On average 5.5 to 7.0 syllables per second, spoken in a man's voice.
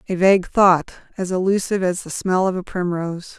No: 5.7 syllables/s; female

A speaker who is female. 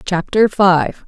Yes: female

